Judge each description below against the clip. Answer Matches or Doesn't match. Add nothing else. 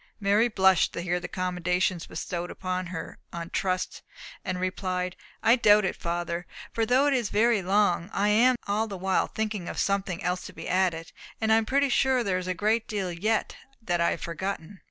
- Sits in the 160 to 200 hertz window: Matches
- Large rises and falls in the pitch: Doesn't match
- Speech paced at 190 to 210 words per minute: Matches